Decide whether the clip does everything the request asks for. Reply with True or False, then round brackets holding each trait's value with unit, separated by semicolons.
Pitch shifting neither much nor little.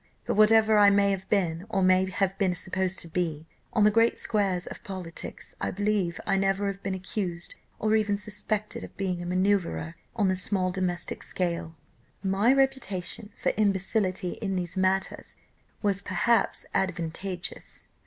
False (2.2 semitones)